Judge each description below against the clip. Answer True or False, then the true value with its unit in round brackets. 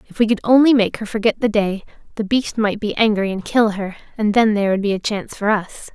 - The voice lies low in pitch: False (210 Hz)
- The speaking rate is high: True (260 wpm)